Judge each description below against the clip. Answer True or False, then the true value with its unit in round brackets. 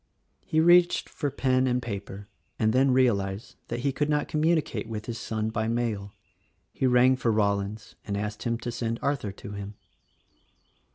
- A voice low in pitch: True (115 Hz)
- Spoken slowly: False (170 wpm)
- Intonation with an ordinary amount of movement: True (3.8 semitones)